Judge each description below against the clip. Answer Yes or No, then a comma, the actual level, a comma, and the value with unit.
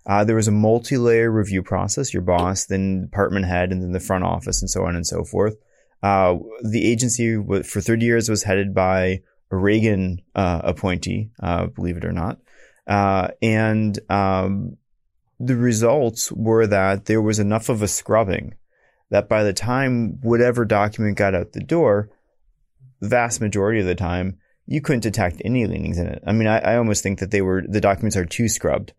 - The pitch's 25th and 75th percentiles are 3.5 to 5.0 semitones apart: No, average, 3.1 semitones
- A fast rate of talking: No, average, 190 wpm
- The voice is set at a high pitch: No, low, 105 Hz